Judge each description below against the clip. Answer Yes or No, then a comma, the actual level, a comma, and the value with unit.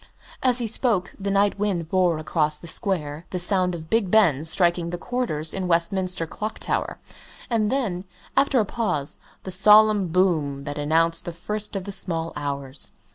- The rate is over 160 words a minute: Yes, average, 175 wpm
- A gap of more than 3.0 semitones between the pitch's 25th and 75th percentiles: Yes, average, 4.1 semitones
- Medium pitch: Yes, medium, 180 Hz